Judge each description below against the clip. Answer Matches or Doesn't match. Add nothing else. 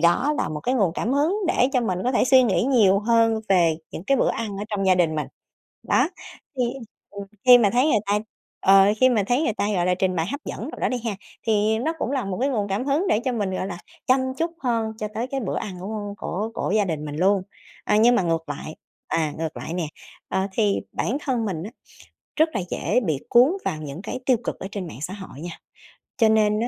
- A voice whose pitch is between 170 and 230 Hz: Matches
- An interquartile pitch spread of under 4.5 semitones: Doesn't match